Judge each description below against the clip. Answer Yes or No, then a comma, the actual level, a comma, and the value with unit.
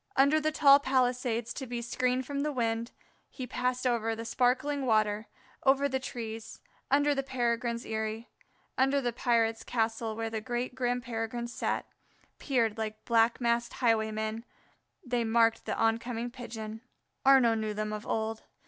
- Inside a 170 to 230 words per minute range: No, average, 155 wpm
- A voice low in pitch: No, high, 235 Hz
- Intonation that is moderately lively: No, narrow, 2.3 semitones